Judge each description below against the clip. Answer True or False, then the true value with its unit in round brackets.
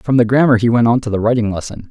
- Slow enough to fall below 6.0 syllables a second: False (7.0 syllables/s)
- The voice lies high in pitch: False (115 Hz)